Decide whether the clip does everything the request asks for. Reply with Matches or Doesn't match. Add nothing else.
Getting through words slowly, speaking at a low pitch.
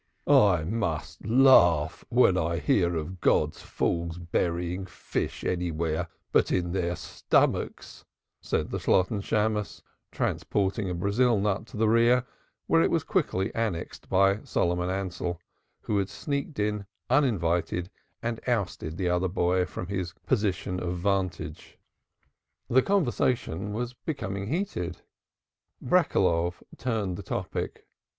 Matches